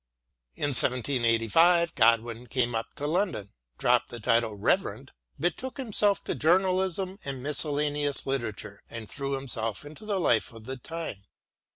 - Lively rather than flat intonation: Yes, wide, 6.6 semitones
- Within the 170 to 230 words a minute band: No, average, 145 wpm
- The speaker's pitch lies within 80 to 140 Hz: Yes, low, 135 Hz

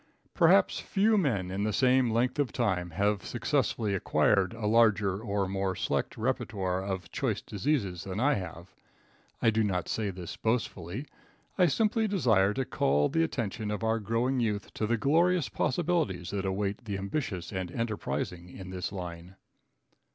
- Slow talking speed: No, average, 160 wpm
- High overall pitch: No, low, 105 Hz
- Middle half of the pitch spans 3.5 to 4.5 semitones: No, average, 4.9 semitones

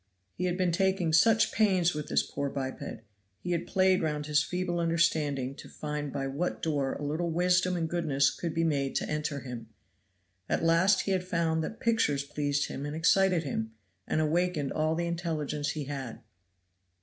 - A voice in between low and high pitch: Yes, medium, 160 Hz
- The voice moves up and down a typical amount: Yes, average, 3.6 semitones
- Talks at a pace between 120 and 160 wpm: No, average, 185 wpm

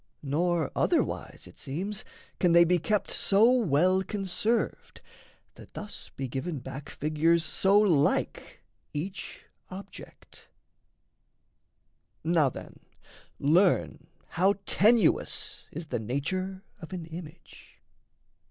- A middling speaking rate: No, slow, 105 wpm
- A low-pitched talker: No, medium, 175 Hz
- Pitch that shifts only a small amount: No, average, 4.3 semitones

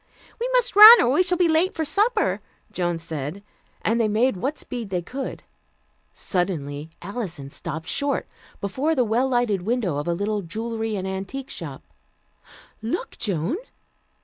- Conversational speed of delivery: Yes, average, 155 wpm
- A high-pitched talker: Yes, high, 220 Hz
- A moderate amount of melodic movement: No, wide, 7.5 semitones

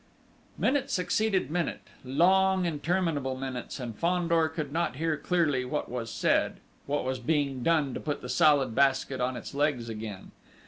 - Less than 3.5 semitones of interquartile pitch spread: No, average, 4.7 semitones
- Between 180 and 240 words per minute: No, average, 155 wpm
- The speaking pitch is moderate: Yes, medium, 145 Hz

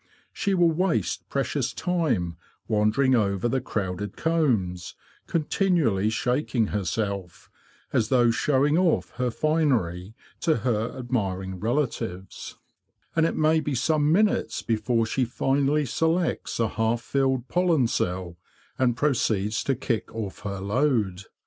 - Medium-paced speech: No, slow, 125 wpm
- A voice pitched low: Yes, low, 120 Hz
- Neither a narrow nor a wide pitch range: No, wide, 6.3 semitones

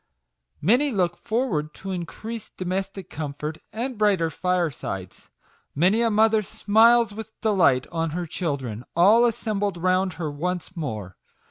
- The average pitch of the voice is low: No, medium, 185 Hz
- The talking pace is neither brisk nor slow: No, slow, 130 wpm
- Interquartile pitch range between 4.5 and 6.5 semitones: Yes, average, 5.2 semitones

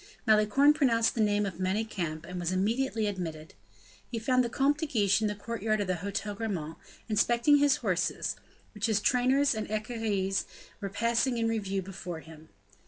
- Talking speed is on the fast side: No, average, 170 wpm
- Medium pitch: No, high, 215 Hz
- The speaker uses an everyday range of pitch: Yes, average, 3.6 semitones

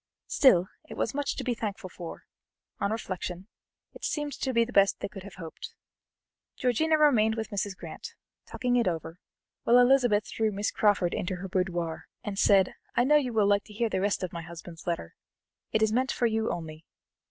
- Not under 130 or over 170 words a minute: No, average, 200 wpm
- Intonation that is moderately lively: Yes, average, 4.6 semitones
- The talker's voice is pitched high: Yes, high, 205 Hz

